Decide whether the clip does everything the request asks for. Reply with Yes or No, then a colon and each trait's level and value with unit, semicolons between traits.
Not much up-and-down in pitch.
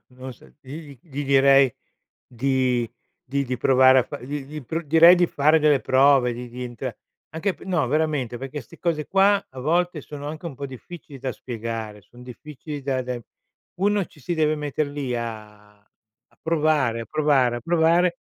No: average, 3.9 semitones